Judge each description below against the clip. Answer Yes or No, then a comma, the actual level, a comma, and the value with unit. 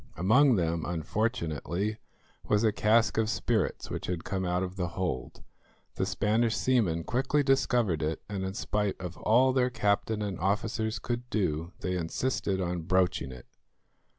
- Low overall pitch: Yes, low, 100 Hz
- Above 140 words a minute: Yes, average, 155 wpm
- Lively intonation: No, average, 4.3 semitones